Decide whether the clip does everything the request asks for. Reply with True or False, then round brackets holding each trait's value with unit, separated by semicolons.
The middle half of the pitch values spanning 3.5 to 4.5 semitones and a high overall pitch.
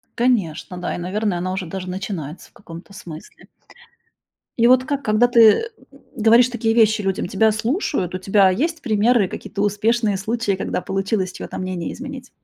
True (4.1 semitones; 210 Hz)